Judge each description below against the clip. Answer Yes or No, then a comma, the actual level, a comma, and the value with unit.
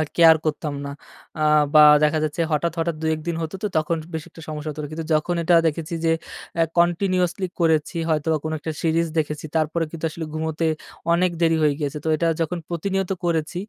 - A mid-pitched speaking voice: Yes, medium, 160 Hz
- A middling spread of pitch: No, narrow, 1.6 semitones